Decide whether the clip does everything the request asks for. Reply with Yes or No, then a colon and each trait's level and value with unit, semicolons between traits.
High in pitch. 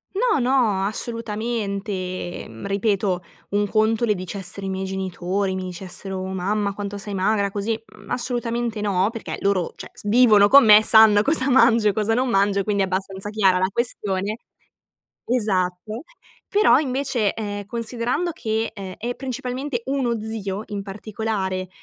Yes: high, 210 Hz